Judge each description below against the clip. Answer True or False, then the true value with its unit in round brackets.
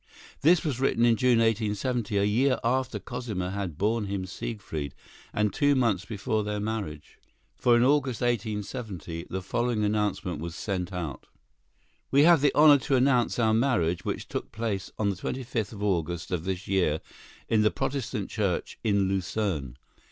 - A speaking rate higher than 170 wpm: False (165 wpm)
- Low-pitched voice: True (105 Hz)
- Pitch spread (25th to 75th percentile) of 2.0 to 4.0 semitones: False (4.4 semitones)